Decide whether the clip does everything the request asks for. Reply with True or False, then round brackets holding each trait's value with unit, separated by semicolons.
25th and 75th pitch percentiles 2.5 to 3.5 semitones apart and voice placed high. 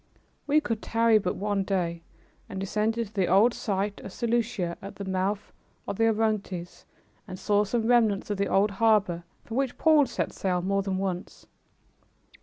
True (2.9 semitones; 205 Hz)